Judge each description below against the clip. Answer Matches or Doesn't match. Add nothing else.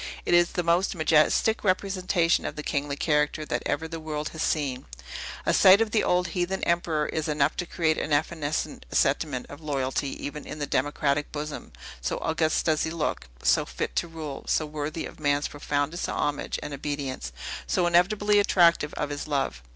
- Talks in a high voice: Doesn't match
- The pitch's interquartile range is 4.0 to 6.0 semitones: Doesn't match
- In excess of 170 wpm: Matches